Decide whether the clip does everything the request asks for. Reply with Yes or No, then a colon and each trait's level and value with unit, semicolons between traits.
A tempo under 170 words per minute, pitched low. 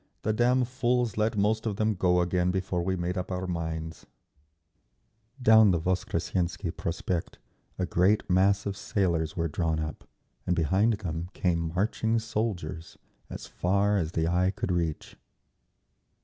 Yes: average, 150 wpm; very low, 90 Hz